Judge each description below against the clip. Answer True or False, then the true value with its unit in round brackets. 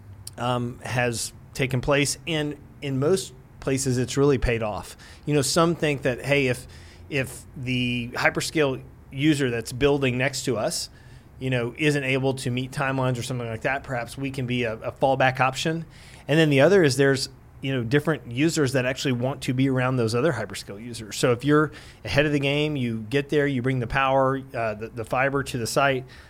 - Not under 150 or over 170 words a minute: False (200 wpm)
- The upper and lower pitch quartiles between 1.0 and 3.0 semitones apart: True (2.7 semitones)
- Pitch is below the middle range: True (130 Hz)